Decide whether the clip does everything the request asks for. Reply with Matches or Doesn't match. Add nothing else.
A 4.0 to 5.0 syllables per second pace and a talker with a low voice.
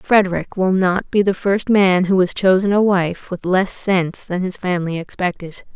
Doesn't match